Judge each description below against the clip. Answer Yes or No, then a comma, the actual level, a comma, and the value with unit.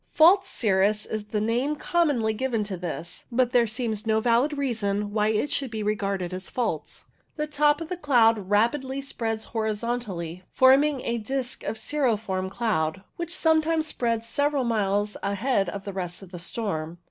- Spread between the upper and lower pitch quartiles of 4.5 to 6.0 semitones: Yes, average, 4.8 semitones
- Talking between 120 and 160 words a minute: No, average, 170 wpm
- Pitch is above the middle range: Yes, high, 225 Hz